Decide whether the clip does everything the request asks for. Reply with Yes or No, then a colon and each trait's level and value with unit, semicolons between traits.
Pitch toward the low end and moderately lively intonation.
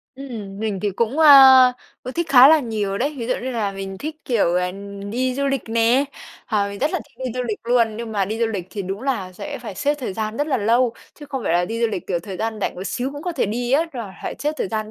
No: high, 235 Hz; average, 4.7 semitones